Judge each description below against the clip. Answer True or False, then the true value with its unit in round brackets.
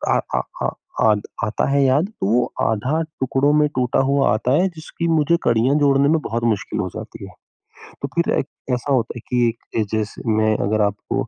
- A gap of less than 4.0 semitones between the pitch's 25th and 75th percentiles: False (4.5 semitones)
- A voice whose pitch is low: True (130 Hz)